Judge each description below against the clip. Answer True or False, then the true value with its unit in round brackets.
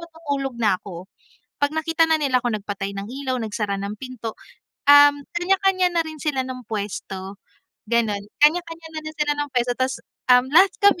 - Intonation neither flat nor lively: False (6.7 semitones)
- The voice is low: False (260 Hz)